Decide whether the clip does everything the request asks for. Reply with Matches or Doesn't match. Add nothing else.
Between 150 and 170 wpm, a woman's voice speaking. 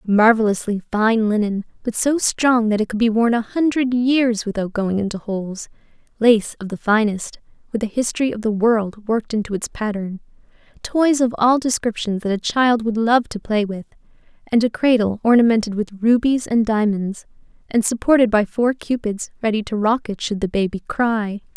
Doesn't match